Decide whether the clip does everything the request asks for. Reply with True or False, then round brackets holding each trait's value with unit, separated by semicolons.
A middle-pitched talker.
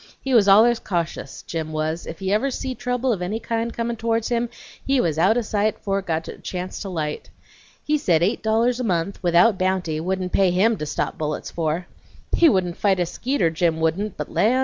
False (195 Hz)